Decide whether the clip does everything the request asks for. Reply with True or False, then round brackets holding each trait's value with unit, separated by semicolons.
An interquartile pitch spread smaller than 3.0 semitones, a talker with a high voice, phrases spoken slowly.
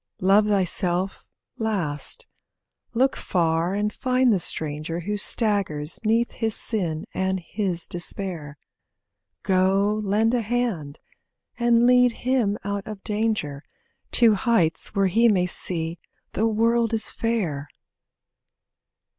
False (4.6 semitones; 200 Hz; 115 wpm)